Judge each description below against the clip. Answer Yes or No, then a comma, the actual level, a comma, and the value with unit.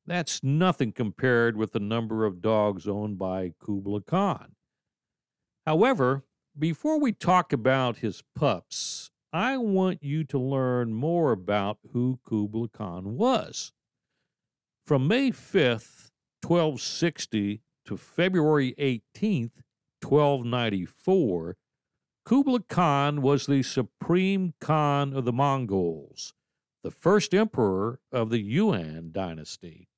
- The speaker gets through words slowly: Yes, slow, 110 wpm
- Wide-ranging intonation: Yes, wide, 7.3 semitones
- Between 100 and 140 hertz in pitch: Yes, low, 135 Hz